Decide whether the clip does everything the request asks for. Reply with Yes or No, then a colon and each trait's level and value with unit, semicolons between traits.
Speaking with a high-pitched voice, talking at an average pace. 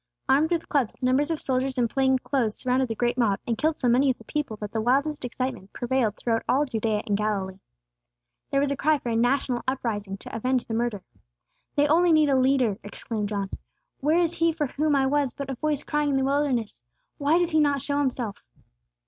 No: very high, 260 Hz; fast, 215 wpm